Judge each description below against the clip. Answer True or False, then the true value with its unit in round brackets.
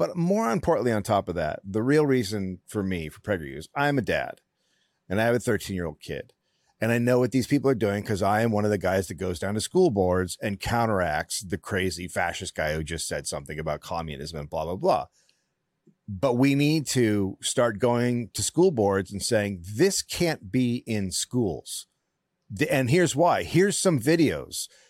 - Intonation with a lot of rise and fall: True (6.5 semitones)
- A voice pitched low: True (110 Hz)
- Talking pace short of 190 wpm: False (200 wpm)